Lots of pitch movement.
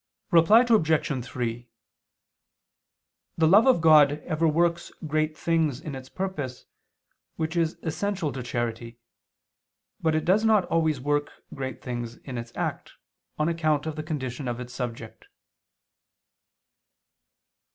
No: average, 4.8 semitones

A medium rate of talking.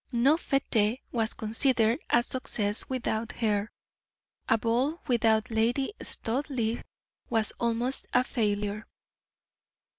No: slow, 100 wpm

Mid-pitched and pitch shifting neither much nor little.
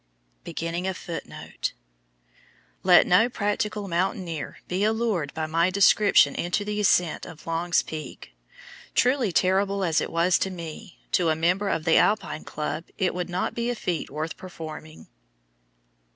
Yes: medium, 180 Hz; average, 3.7 semitones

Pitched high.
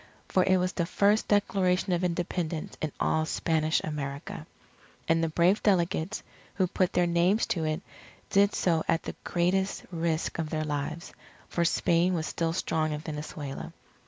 No: medium, 170 Hz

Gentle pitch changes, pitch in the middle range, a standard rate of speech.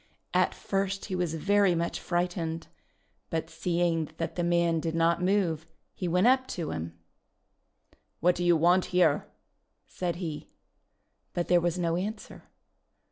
Yes: narrow, 1.7 semitones; medium, 175 Hz; average, 145 wpm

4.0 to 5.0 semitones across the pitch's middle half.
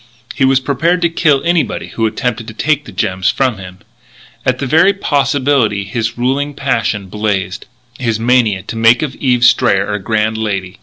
Yes: average, 4.6 semitones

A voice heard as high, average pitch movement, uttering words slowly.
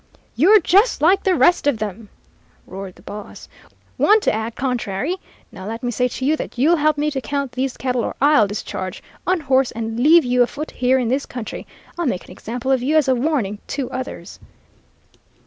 No: very high, 260 Hz; average, 4.7 semitones; average, 200 wpm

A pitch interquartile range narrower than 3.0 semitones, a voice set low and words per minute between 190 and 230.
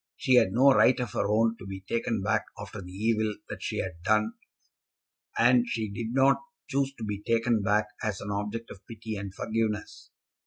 Yes: narrow, 2.4 semitones; low, 110 Hz; average, 195 wpm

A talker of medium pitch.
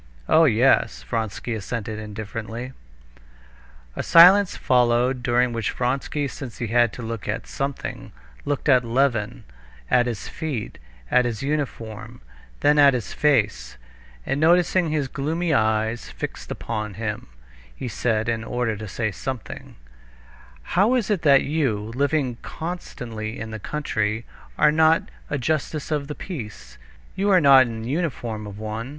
No: low, 125 Hz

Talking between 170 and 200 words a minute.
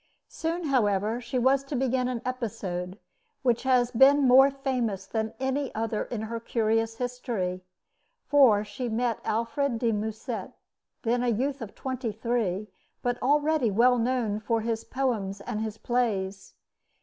No: average, 150 wpm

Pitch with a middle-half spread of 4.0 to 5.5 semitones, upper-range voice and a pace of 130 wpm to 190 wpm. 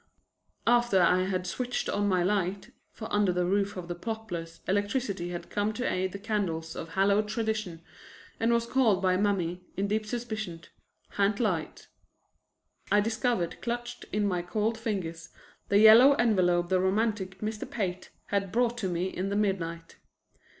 No: average, 3.4 semitones; high, 200 Hz; average, 160 wpm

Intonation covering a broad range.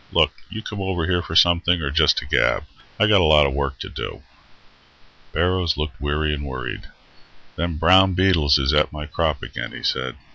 No: average, 3.5 semitones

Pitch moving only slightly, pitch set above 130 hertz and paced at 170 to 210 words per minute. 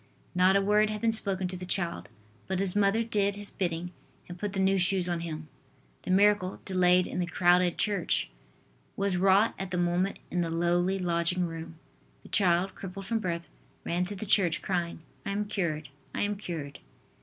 Yes: narrow, 2.3 semitones; medium, 185 Hz; average, 190 wpm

